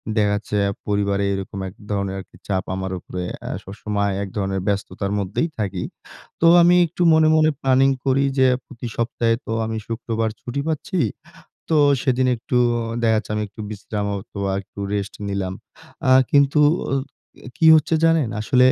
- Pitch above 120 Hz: No, low, 110 Hz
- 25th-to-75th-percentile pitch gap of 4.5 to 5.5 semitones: Yes, average, 5.1 semitones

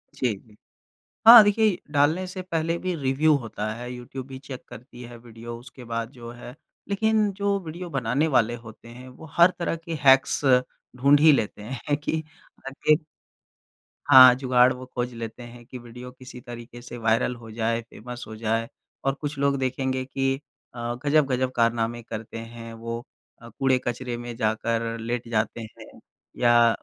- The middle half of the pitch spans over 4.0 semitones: No, average, 3.2 semitones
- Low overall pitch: Yes, low, 125 Hz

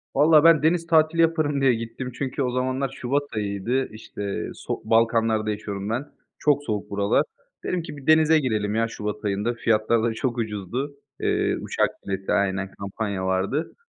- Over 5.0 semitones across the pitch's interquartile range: Yes, wide, 5.5 semitones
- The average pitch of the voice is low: Yes, low, 115 Hz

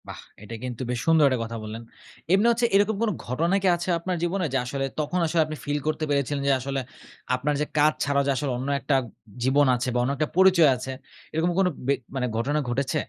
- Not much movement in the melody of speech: No, average, 4.6 semitones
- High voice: No, medium, 145 Hz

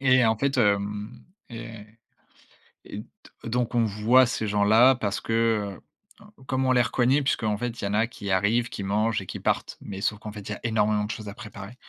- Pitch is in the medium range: No, low, 110 Hz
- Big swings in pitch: No, average, 2.9 semitones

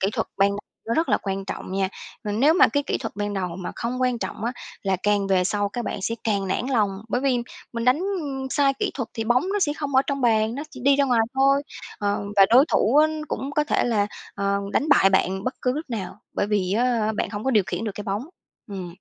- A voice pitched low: No, high, 225 Hz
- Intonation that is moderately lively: Yes, average, 4.8 semitones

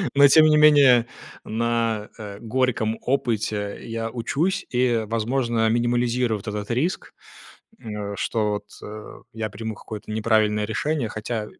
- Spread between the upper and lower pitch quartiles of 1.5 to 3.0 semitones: Yes, narrow, 2.6 semitones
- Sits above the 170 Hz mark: No, low, 115 Hz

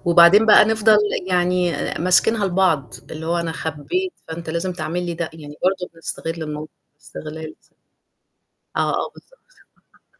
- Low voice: No, medium, 170 Hz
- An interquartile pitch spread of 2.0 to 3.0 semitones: Yes, narrow, 2.6 semitones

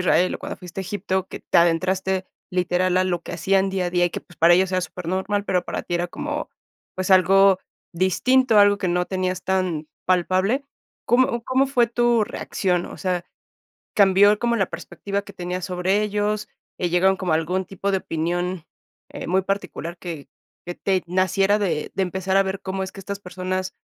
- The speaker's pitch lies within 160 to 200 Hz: Yes, medium, 185 Hz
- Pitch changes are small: Yes, narrow, 1.7 semitones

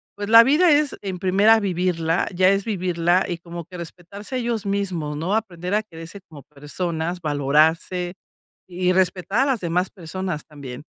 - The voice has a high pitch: No, medium, 180 Hz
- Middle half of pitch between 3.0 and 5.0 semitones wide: Yes, average, 3.3 semitones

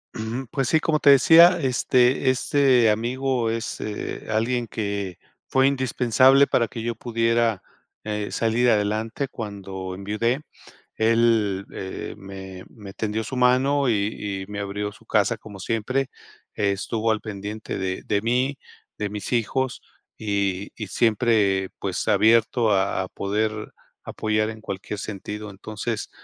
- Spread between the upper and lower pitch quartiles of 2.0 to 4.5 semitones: Yes, average, 3.2 semitones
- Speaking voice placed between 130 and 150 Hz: No, low, 110 Hz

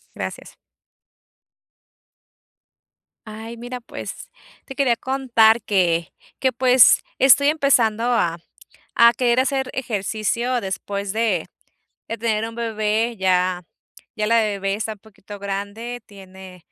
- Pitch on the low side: No, high, 225 Hz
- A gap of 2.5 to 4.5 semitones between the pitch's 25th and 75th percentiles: Yes, average, 3.4 semitones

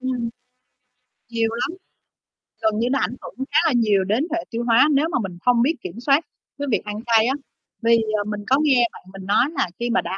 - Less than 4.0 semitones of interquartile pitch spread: Yes, average, 3.5 semitones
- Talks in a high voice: Yes, high, 235 Hz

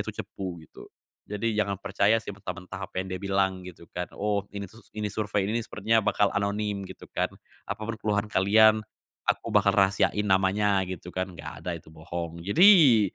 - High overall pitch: No, low, 100 Hz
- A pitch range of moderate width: No, narrow, 2.2 semitones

